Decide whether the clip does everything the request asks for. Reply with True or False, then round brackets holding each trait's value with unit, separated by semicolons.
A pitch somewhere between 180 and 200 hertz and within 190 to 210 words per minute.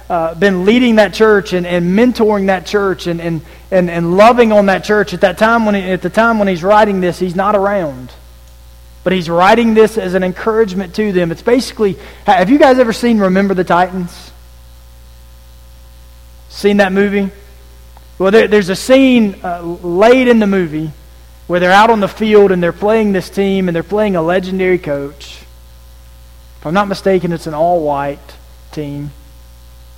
False (185 Hz; 180 wpm)